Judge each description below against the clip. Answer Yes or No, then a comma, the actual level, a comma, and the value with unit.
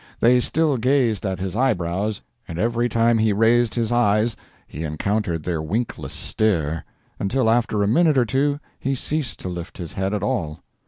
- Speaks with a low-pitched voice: Yes, low, 110 Hz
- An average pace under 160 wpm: No, average, 170 wpm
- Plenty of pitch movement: No, average, 4.6 semitones